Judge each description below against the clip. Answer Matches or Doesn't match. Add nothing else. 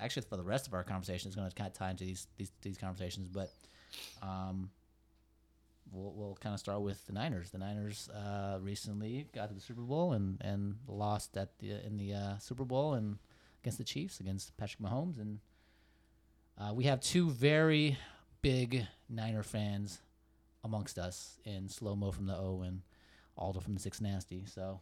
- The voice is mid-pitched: Doesn't match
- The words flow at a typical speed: Matches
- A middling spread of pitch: Doesn't match